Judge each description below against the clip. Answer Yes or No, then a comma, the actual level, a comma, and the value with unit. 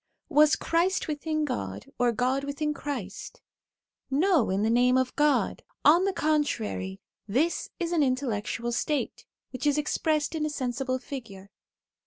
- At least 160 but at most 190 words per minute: No, average, 145 wpm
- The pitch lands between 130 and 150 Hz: No, very high, 275 Hz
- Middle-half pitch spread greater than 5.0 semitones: No, average, 4.2 semitones